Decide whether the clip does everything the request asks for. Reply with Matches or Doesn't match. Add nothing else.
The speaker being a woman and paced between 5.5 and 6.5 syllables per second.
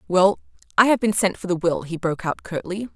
Matches